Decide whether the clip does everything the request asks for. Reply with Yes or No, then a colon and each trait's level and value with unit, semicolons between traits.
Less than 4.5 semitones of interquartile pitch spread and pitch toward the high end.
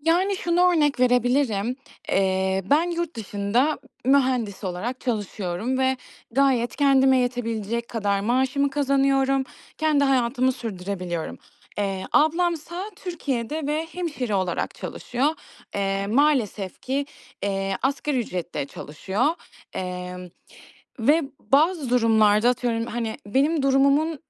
No: wide, 5.6 semitones; very high, 250 Hz